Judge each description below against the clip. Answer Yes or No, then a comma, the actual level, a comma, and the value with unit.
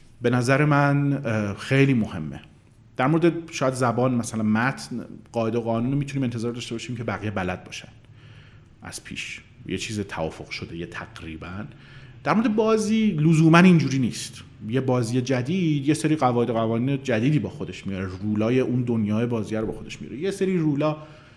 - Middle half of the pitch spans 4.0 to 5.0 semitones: Yes, average, 4.5 semitones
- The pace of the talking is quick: Yes, fast, 160 wpm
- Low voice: Yes, low, 120 Hz